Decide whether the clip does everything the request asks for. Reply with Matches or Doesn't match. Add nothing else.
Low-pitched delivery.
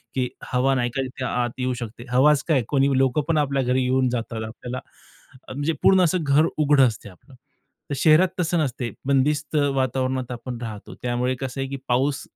Matches